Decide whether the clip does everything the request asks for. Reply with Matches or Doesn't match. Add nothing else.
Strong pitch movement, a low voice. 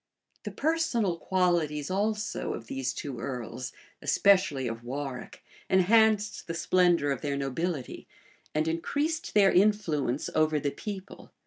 Doesn't match